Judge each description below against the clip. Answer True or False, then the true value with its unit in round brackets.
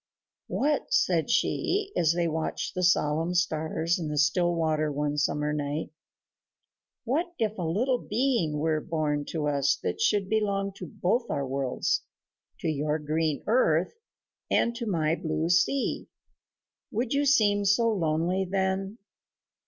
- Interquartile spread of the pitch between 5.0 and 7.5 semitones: True (5.5 semitones)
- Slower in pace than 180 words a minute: True (145 wpm)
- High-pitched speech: False (170 Hz)